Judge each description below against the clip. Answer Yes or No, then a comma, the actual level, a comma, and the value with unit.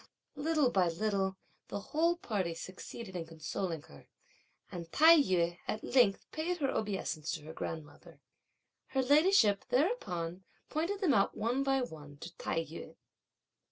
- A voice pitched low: No, high, 200 Hz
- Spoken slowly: No, average, 145 wpm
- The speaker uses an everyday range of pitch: No, wide, 8.9 semitones